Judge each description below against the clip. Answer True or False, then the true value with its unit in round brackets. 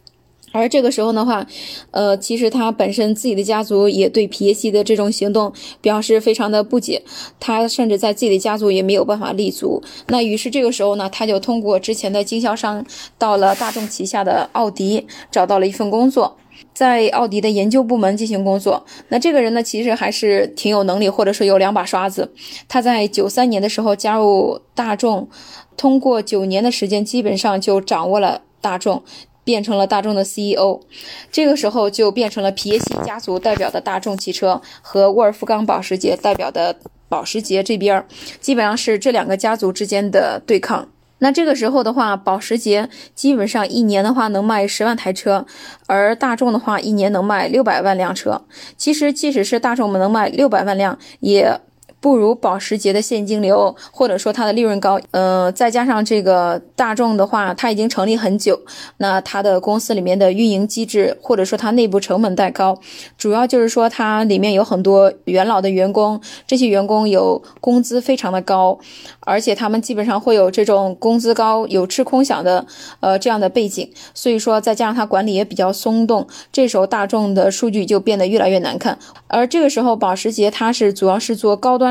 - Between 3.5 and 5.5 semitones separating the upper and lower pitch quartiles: False (2.9 semitones)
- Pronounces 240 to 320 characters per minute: True (300 characters per minute)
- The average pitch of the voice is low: False (215 Hz)